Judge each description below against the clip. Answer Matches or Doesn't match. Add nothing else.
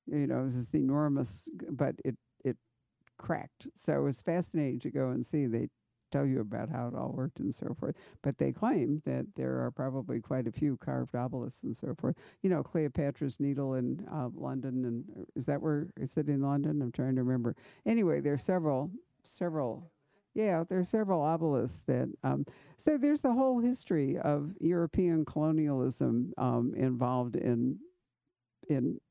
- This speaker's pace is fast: Doesn't match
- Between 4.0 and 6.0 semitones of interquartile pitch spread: Matches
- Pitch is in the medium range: Matches